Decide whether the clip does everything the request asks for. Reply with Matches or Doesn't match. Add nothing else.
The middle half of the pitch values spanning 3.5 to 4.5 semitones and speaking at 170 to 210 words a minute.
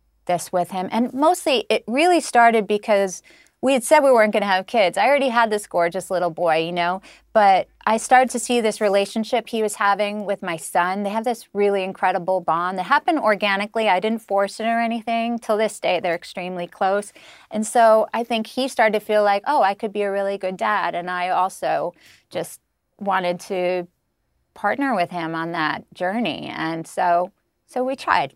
Matches